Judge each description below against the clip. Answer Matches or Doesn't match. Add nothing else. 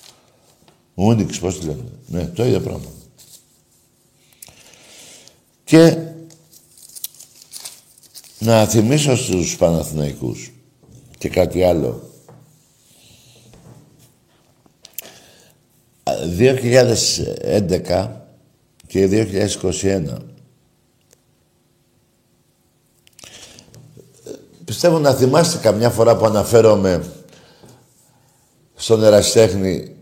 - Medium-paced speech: Doesn't match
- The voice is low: Matches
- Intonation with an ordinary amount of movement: Doesn't match